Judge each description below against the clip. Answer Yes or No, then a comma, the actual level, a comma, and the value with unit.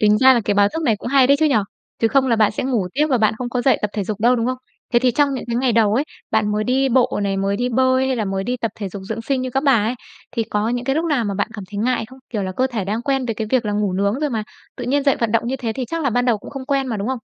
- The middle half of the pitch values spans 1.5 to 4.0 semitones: Yes, average, 3.7 semitones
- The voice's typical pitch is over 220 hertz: Yes, high, 240 Hz